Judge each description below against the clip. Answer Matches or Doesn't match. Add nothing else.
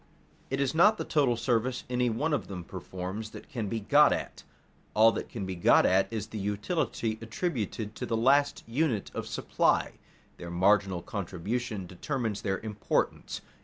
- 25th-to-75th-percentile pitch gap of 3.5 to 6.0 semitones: Matches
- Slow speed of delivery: Doesn't match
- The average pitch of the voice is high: Doesn't match